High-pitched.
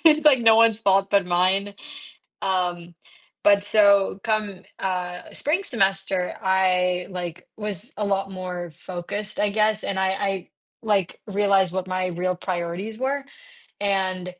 Yes: high, 195 Hz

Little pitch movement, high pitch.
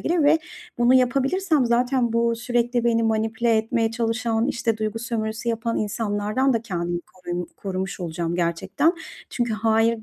Yes: narrow, 2.0 semitones; high, 230 Hz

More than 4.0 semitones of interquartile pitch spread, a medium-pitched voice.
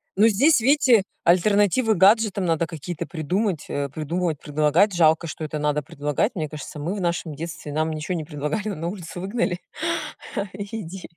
Yes: average, 4.8 semitones; medium, 170 Hz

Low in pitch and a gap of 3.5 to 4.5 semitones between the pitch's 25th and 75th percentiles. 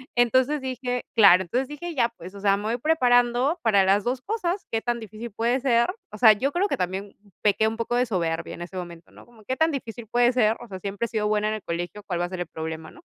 No: high, 225 Hz; average, 4.1 semitones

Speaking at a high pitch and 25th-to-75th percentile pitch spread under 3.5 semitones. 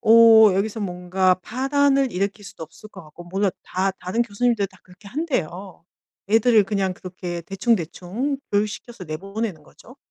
No: high, 200 Hz; average, 3.8 semitones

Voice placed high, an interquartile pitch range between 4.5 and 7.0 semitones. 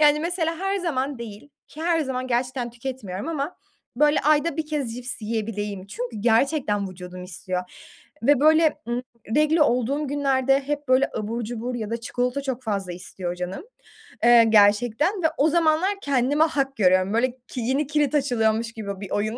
Yes: very high, 250 Hz; average, 5.1 semitones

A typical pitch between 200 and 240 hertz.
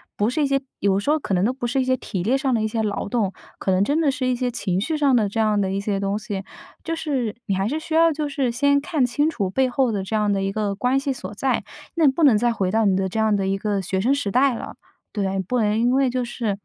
Yes: high, 230 Hz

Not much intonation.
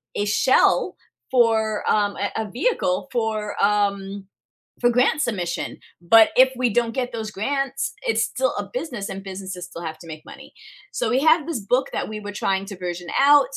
No: average, 4.9 semitones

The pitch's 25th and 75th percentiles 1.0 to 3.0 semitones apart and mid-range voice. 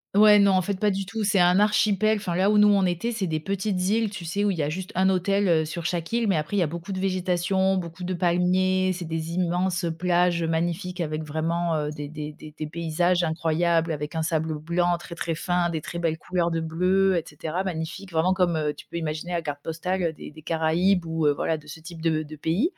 Yes: narrow, 2.6 semitones; medium, 175 Hz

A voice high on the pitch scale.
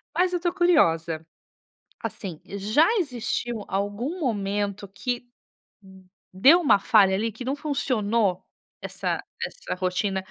Yes: high, 210 Hz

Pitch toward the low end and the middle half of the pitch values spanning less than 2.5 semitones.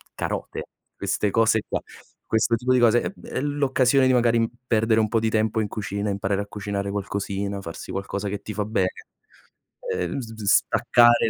No: low, 110 Hz; average, 2.8 semitones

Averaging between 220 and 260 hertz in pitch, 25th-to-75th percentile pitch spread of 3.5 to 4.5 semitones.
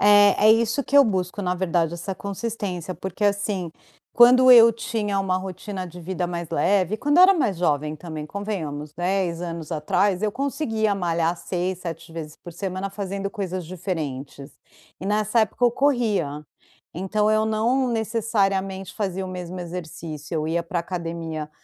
No: high, 190 Hz; average, 3.9 semitones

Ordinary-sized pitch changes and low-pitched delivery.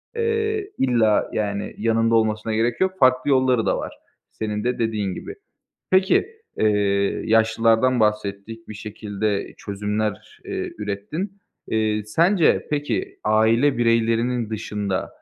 Yes: average, 3.1 semitones; low, 110 Hz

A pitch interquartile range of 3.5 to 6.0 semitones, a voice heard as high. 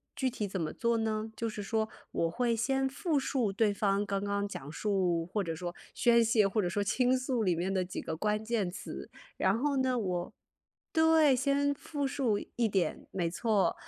Yes: average, 4.7 semitones; high, 215 Hz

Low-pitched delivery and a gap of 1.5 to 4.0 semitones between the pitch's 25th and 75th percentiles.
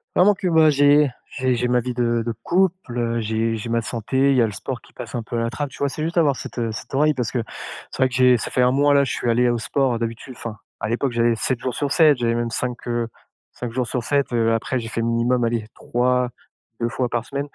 Yes: low, 125 Hz; average, 2.8 semitones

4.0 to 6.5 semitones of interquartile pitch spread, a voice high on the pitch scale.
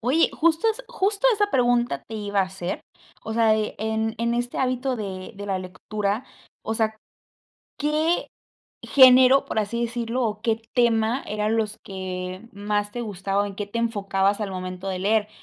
No: average, 3.3 semitones; high, 220 Hz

